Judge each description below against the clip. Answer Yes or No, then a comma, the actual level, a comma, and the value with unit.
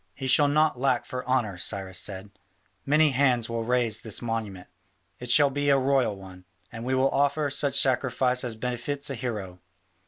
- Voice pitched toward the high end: No, low, 125 Hz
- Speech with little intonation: No, average, 3.8 semitones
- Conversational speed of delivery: Yes, average, 180 wpm